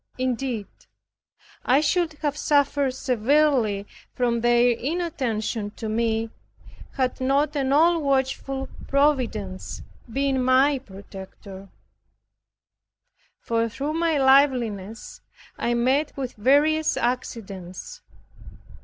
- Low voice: No, very high, 255 Hz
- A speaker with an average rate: No, slow, 90 wpm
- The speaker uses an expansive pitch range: No, average, 3.9 semitones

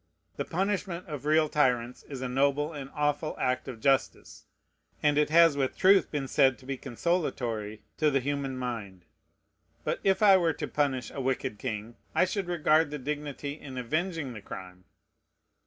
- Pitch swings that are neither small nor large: Yes, average, 3.5 semitones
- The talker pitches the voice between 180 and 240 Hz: No, medium, 140 Hz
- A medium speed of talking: Yes, average, 170 wpm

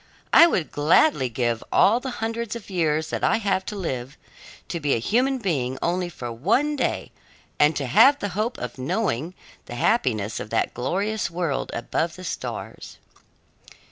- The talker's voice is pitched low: No, medium, 170 Hz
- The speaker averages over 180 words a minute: No, average, 170 wpm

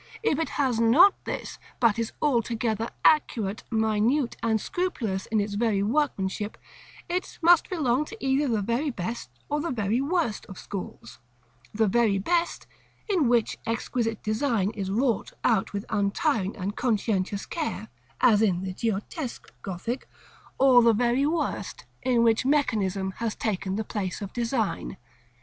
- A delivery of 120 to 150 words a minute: Yes, average, 145 wpm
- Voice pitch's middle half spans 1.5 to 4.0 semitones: No, average, 4.6 semitones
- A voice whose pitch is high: Yes, high, 230 Hz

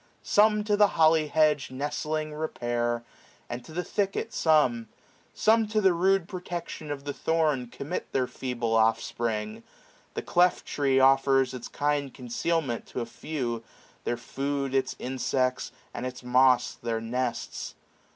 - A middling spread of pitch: Yes, average, 4.5 semitones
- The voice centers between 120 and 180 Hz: Yes, low, 135 Hz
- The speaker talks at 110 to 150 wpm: Yes, average, 145 wpm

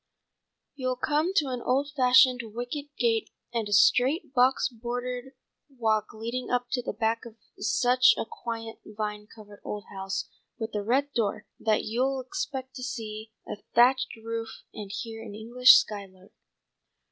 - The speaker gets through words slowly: No, average, 155 wpm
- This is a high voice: Yes, high, 235 Hz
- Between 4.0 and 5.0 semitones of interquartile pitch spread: No, average, 2.8 semitones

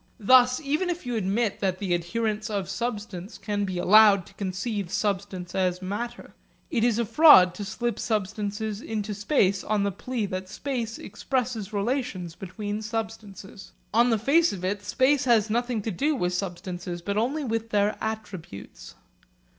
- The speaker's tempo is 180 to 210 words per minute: No, average, 160 wpm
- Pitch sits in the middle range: No, high, 210 Hz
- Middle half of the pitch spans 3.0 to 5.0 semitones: Yes, average, 3.5 semitones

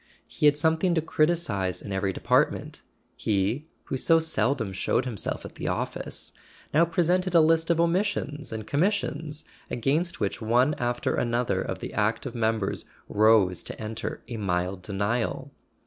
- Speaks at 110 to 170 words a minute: Yes, average, 160 wpm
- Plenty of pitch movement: Yes, wide, 7.1 semitones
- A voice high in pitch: No, low, 125 Hz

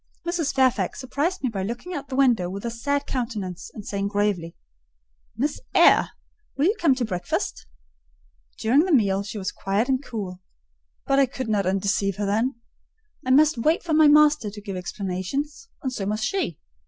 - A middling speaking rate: Yes, average, 180 wpm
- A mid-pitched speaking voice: No, high, 225 Hz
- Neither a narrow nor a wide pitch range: No, wide, 6.2 semitones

